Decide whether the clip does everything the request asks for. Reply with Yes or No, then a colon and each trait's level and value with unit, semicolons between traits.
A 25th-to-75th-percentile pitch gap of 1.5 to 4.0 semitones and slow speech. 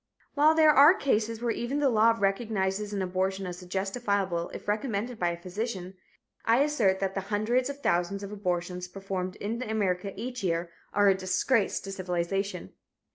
No: average, 3.7 semitones; average, 170 wpm